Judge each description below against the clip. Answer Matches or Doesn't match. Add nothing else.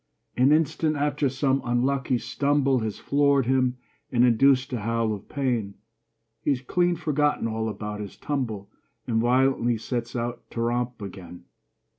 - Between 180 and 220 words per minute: Doesn't match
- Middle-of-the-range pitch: Doesn't match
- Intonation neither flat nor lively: Matches